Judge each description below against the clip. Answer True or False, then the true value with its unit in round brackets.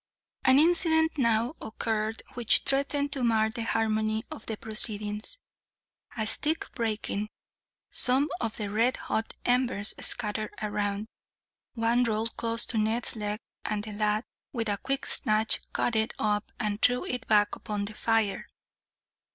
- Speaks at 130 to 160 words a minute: True (145 wpm)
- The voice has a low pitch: False (220 Hz)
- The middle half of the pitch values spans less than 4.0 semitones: True (2.4 semitones)